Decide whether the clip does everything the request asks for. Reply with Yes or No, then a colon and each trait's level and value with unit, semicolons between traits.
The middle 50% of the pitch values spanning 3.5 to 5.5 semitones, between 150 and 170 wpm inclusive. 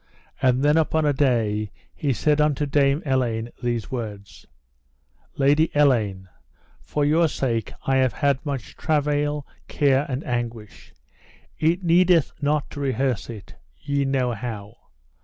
No: average, 3.8 semitones; slow, 135 wpm